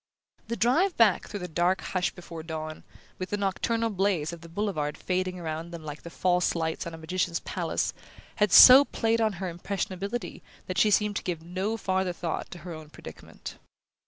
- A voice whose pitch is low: No, medium, 180 Hz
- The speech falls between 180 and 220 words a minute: Yes, average, 190 wpm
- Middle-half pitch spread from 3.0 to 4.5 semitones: Yes, average, 3.6 semitones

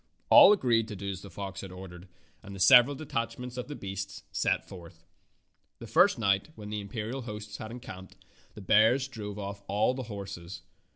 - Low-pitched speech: Yes, low, 105 Hz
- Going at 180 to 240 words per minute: Yes, average, 185 wpm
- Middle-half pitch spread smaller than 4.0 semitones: Yes, average, 3.5 semitones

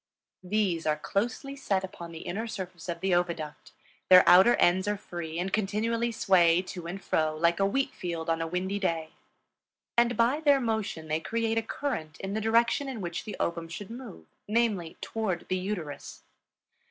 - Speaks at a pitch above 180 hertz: Yes, high, 190 Hz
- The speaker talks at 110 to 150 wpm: No, average, 180 wpm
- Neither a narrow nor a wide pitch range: Yes, average, 4.8 semitones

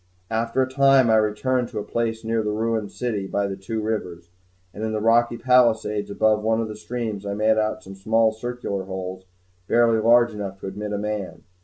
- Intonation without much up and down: Yes, narrow, 2.1 semitones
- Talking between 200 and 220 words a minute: Yes, fast, 205 wpm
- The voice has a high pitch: No, low, 110 Hz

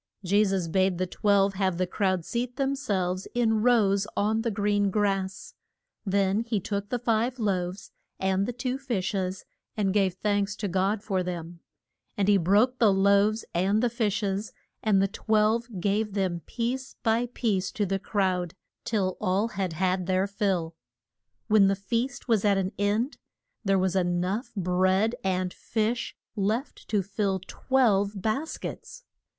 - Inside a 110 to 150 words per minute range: No, average, 165 wpm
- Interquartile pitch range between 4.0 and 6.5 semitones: No, average, 2.7 semitones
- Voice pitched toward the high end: Yes, high, 200 Hz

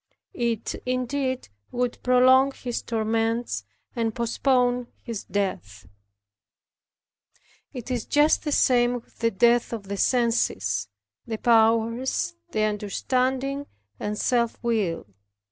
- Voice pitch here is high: Yes, high, 235 Hz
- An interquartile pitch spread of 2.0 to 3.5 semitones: Yes, narrow, 2.5 semitones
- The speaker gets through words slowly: Yes, slow, 110 wpm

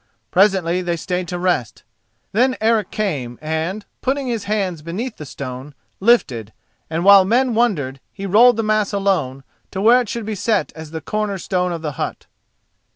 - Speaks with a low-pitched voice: No, high, 190 Hz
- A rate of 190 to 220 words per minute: No, average, 175 wpm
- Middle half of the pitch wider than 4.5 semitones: Yes, average, 5.1 semitones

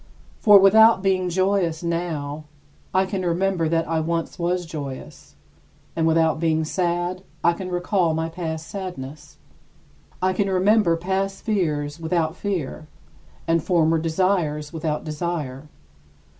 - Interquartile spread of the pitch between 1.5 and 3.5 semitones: Yes, average, 2.9 semitones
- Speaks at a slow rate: Yes, slow, 130 wpm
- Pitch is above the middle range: No, medium, 170 Hz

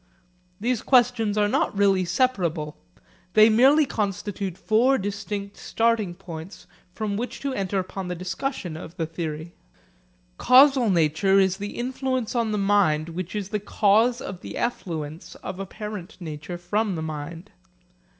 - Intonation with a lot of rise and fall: No, average, 4.2 semitones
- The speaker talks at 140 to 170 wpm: Yes, average, 145 wpm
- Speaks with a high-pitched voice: Yes, high, 200 Hz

